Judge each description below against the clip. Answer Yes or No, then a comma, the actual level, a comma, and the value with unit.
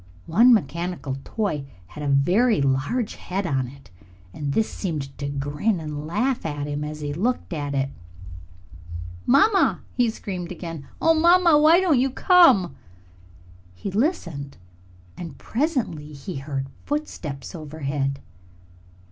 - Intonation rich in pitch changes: Yes, wide, 9.0 semitones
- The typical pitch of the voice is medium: Yes, medium, 165 Hz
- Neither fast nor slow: No, slow, 130 wpm